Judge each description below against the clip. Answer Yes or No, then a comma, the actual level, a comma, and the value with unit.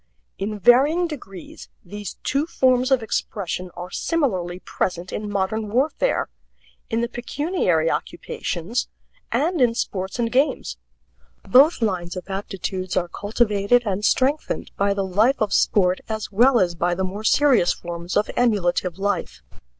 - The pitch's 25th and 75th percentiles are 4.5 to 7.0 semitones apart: Yes, average, 5.2 semitones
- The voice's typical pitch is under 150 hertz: No, high, 205 Hz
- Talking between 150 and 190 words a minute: No, average, 140 wpm